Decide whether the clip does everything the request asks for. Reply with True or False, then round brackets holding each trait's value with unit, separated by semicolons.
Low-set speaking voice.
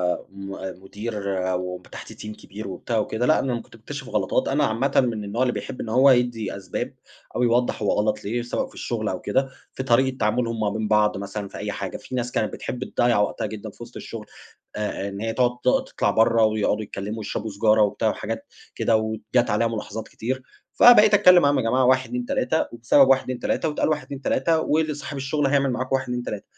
True (120 Hz)